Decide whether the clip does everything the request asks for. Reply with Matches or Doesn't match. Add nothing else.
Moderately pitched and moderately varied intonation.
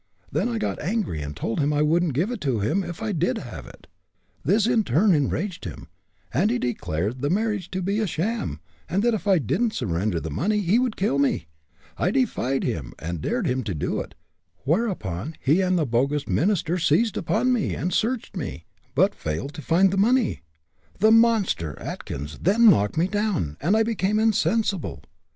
Doesn't match